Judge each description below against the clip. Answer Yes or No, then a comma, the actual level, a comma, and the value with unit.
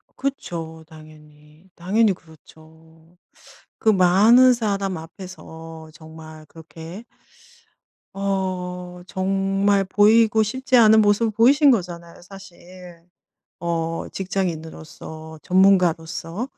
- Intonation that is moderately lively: Yes, average, 3.7 semitones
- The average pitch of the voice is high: No, medium, 180 Hz